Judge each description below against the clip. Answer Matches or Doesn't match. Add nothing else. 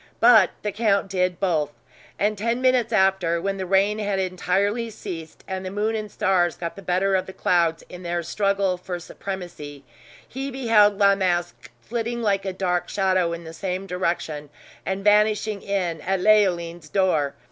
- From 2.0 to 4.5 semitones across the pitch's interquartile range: Matches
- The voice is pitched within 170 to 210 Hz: Matches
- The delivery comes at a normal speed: Matches